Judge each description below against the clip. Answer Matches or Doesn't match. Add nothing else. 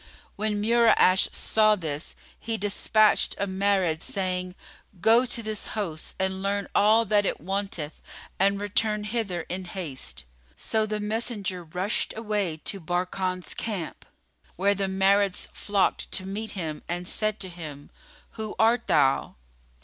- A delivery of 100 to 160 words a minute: Matches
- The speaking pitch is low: Doesn't match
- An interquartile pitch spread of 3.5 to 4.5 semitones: Doesn't match